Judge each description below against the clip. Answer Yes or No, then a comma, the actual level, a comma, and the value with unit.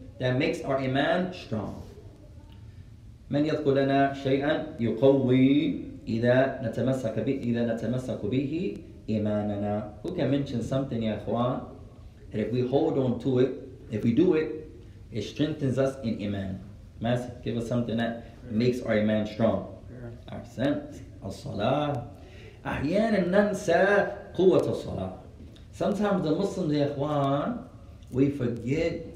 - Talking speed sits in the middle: No, slow, 130 wpm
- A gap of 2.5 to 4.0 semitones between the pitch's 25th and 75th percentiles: No, average, 4.7 semitones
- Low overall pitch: Yes, low, 120 Hz